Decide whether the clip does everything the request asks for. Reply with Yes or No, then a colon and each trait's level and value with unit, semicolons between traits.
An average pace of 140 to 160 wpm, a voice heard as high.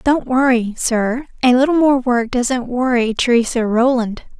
Yes: average, 150 wpm; high, 245 Hz